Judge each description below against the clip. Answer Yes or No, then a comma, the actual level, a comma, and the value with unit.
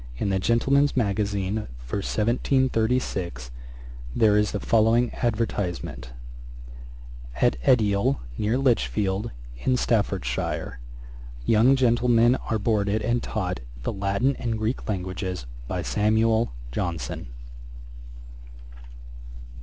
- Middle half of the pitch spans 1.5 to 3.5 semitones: Yes, average, 3.2 semitones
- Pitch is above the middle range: No, low, 110 Hz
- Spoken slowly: Yes, slow, 95 wpm